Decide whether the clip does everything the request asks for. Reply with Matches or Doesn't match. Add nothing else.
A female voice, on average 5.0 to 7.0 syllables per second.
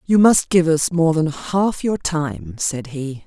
Doesn't match